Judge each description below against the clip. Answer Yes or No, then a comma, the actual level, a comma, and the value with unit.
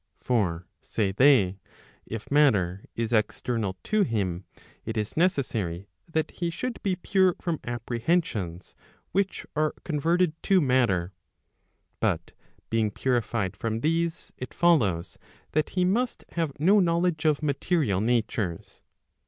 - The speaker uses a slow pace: Yes, slow, 130 wpm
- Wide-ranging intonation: Yes, wide, 8.4 semitones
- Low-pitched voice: Yes, low, 125 Hz